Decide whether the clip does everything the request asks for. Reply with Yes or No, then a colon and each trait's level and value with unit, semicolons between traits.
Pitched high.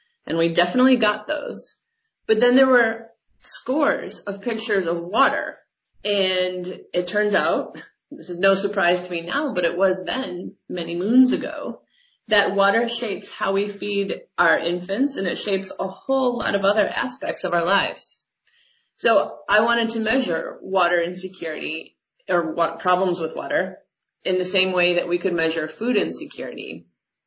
Yes: high, 195 Hz